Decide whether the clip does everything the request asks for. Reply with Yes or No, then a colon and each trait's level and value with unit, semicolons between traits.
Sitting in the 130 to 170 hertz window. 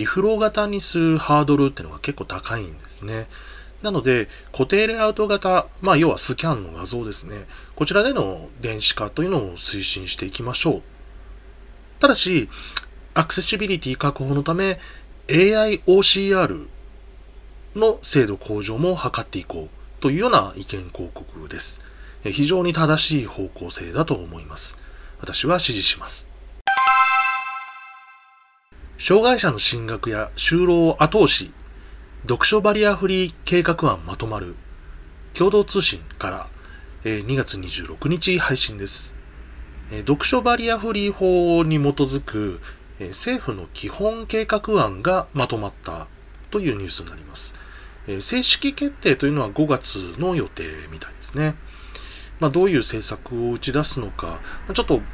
Yes: medium, 140 Hz